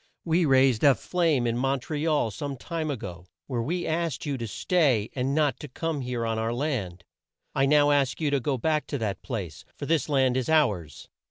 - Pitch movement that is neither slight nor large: Yes, average, 4.5 semitones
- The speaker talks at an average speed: No, fast, 220 wpm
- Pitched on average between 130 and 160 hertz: Yes, low, 135 Hz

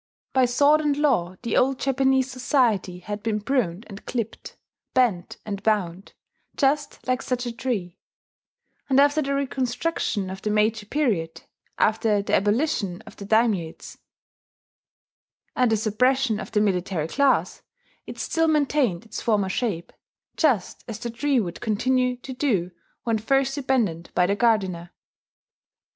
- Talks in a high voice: Yes, high, 230 Hz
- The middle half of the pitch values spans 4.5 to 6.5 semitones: Yes, average, 4.9 semitones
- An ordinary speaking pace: Yes, average, 145 wpm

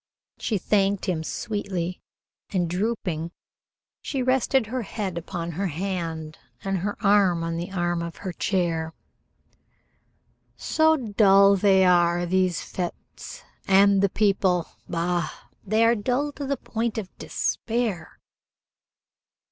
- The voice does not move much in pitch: No, average, 3.5 semitones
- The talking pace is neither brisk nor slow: No, slow, 125 wpm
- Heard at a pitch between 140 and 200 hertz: Yes, high, 190 Hz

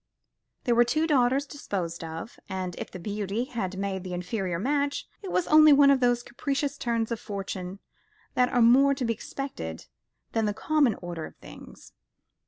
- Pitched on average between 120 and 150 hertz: No, high, 235 Hz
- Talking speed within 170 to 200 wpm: Yes, average, 180 wpm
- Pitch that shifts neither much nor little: No, wide, 6.5 semitones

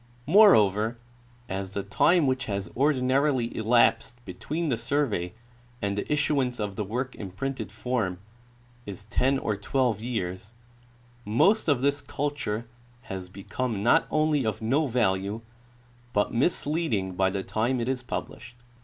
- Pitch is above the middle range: No, low, 120 Hz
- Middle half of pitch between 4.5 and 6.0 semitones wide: Yes, average, 5.0 semitones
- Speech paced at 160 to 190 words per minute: No, average, 140 wpm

